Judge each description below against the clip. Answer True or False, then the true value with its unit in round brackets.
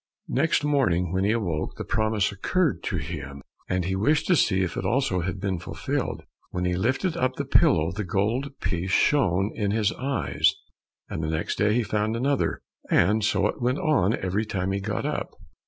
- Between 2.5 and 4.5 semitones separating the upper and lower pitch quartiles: False (5.2 semitones)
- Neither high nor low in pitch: False (105 Hz)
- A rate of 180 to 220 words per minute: True (190 wpm)